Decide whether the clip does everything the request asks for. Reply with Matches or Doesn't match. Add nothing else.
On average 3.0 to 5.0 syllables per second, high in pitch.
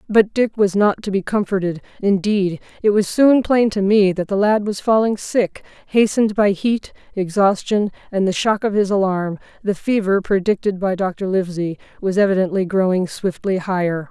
Matches